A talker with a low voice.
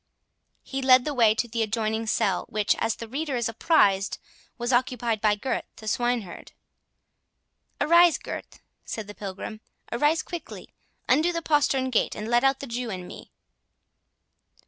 No: high, 240 Hz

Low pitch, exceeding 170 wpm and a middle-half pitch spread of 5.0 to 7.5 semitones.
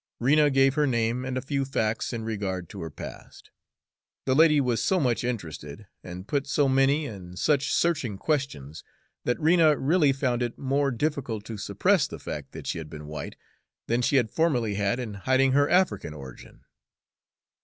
Yes: low, 125 Hz; average, 180 wpm; wide, 5.5 semitones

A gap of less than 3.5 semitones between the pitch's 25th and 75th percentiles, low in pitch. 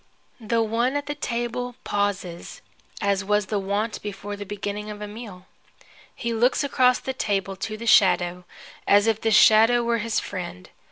No: narrow, 2.6 semitones; high, 210 Hz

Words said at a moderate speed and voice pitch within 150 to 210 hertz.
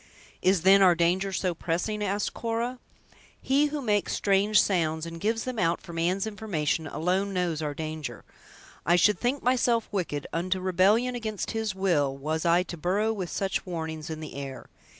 Yes: average, 175 wpm; medium, 185 Hz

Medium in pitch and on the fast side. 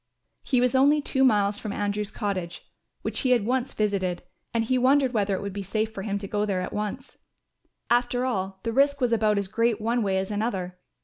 No: high, 215 Hz; fast, 220 wpm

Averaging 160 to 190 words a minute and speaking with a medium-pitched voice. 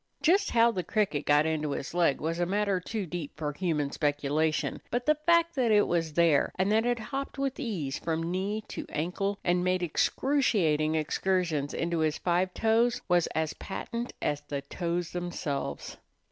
Yes: average, 175 wpm; medium, 175 Hz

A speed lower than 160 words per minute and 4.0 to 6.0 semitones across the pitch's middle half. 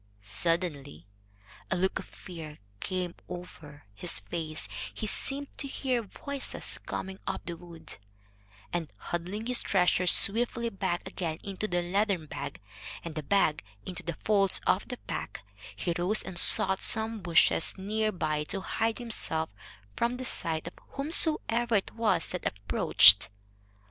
Yes: average, 145 wpm; average, 4.8 semitones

